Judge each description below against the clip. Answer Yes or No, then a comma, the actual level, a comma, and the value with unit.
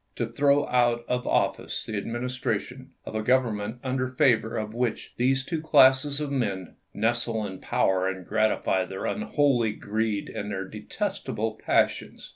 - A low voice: Yes, low, 120 Hz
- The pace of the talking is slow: No, average, 160 wpm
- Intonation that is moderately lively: Yes, average, 3.6 semitones